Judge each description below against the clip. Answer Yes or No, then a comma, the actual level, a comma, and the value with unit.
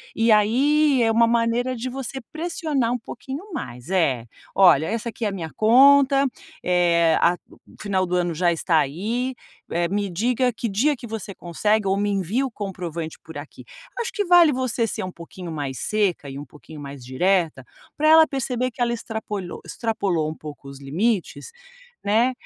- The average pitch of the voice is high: Yes, high, 210 Hz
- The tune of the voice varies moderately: No, wide, 6.6 semitones